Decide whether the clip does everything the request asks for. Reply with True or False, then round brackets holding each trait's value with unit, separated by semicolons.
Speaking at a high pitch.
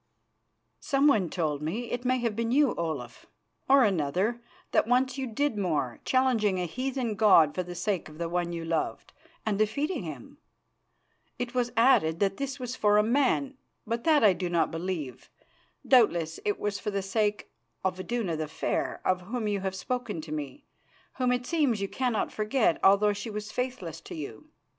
True (210 Hz)